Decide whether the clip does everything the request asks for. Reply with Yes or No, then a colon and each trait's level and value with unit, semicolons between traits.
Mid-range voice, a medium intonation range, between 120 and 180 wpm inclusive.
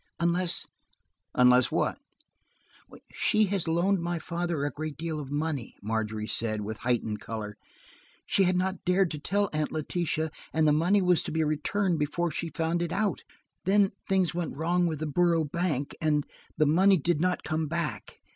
Yes: medium, 165 Hz; average, 3.3 semitones; average, 165 wpm